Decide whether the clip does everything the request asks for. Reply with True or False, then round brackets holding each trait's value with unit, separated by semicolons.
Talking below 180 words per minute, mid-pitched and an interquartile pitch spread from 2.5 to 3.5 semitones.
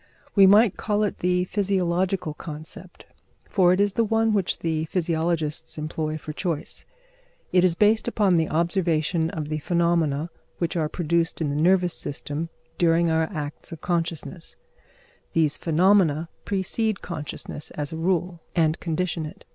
True (150 wpm; 170 Hz; 2.9 semitones)